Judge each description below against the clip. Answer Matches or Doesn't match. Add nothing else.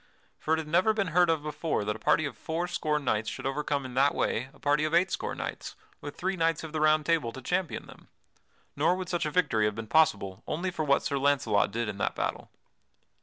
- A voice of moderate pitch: Matches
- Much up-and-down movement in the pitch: Doesn't match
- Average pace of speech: Doesn't match